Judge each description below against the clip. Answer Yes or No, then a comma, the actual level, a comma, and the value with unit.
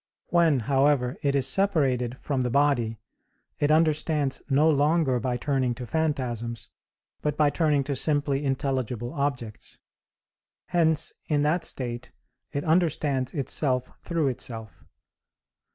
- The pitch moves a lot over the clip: No, average, 3.3 semitones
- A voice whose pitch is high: No, medium, 140 Hz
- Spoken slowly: Yes, slow, 120 wpm